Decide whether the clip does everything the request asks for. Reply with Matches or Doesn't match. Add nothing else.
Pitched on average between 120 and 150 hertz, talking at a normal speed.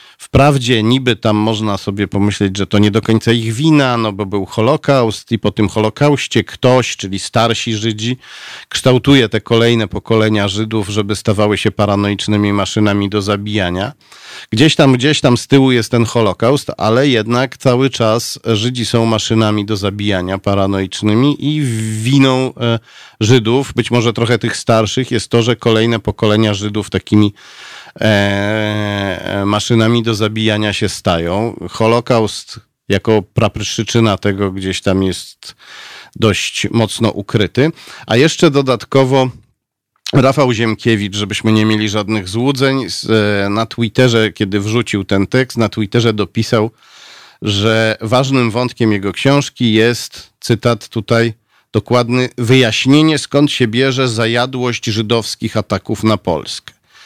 Doesn't match